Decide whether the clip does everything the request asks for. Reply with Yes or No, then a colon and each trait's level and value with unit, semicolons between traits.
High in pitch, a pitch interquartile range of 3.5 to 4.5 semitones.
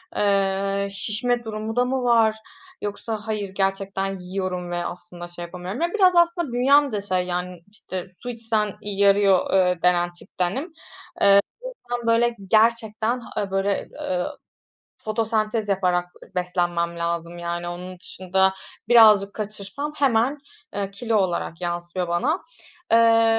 Yes: high, 200 Hz; average, 4.0 semitones